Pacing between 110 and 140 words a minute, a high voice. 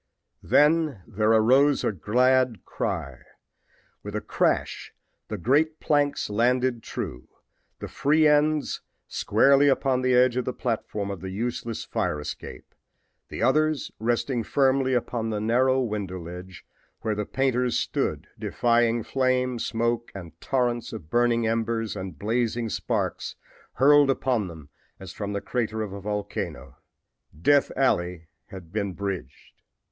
No: slow, 135 wpm; low, 115 Hz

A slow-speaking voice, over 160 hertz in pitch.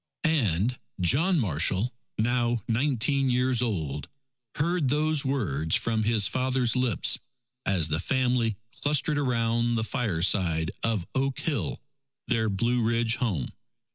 No: slow, 120 wpm; low, 120 Hz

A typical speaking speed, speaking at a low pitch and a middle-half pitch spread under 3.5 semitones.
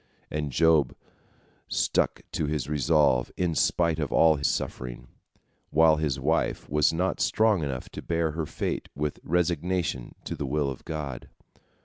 Yes: average, 150 wpm; very low, 75 Hz; narrow, 2.6 semitones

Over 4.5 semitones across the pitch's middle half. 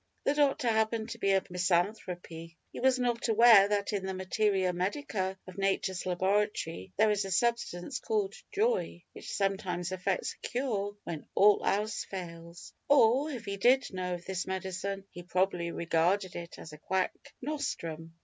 No: average, 3.9 semitones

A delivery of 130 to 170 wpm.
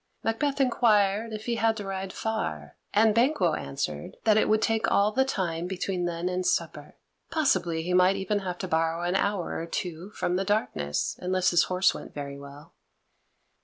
No: average, 185 wpm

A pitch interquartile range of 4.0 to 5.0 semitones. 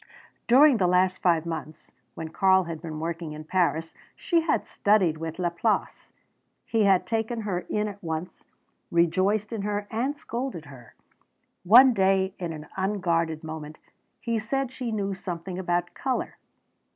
Yes: average, 4.6 semitones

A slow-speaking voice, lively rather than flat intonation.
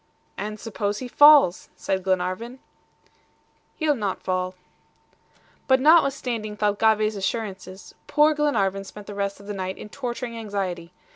No: slow, 130 wpm; average, 4.3 semitones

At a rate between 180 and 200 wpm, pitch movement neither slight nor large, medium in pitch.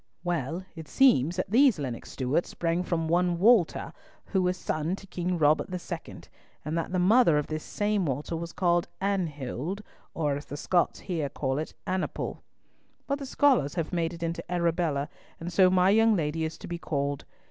Yes: average, 185 wpm; average, 3.4 semitones; medium, 170 Hz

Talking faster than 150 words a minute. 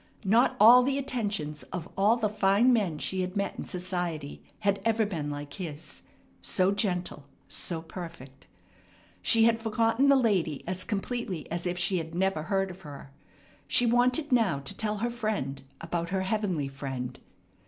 Yes: average, 165 wpm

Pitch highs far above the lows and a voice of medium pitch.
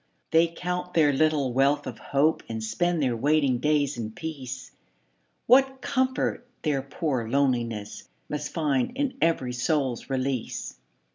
No: average, 4.1 semitones; medium, 145 Hz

